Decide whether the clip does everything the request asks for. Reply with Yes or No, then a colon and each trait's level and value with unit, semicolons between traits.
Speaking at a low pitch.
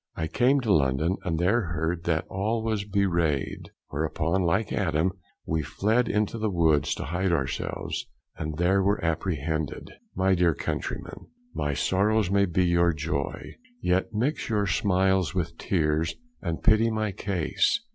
Yes: very low, 90 Hz